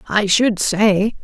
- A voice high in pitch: Yes, high, 205 Hz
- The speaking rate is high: No, average, 145 wpm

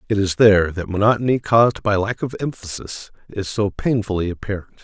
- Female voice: No, male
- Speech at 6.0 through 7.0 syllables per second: No, 5.8 syllables/s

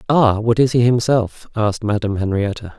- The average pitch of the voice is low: Yes, low, 110 Hz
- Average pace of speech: Yes, average, 170 wpm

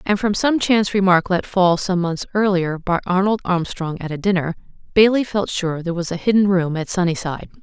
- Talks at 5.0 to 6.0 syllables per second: Yes, 5.5 syllables/s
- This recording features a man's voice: No, female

